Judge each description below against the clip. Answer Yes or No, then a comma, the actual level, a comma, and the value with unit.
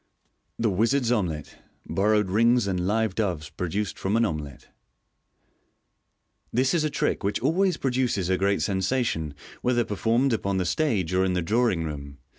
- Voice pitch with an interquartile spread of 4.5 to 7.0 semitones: Yes, average, 4.8 semitones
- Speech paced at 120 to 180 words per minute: Yes, average, 165 wpm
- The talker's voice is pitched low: Yes, low, 105 Hz